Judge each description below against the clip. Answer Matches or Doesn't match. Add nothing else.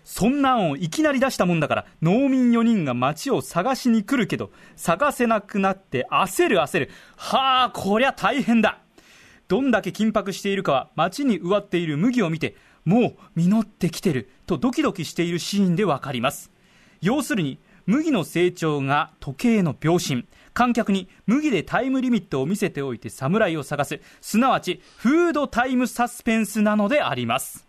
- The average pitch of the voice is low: Doesn't match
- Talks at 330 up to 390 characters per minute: Matches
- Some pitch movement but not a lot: Doesn't match